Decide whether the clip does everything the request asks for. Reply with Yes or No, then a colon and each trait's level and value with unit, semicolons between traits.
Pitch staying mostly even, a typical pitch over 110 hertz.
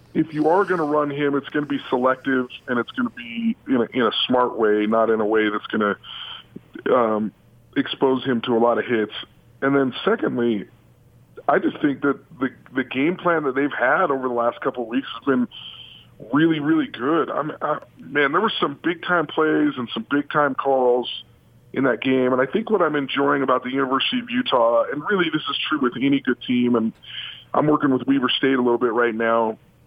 No: average, 3.8 semitones; low, 135 Hz